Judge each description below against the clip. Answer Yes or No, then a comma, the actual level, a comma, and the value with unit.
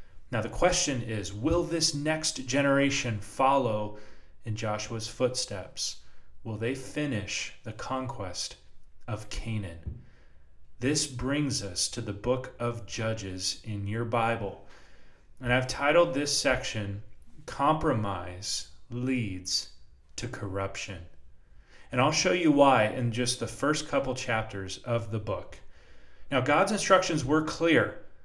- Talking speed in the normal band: No, slow, 125 wpm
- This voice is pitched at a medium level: No, low, 115 Hz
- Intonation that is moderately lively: No, wide, 5.7 semitones